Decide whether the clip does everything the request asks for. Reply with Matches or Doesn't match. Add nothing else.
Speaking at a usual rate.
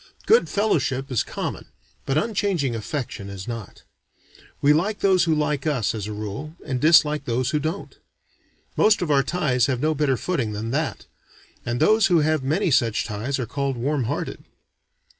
Matches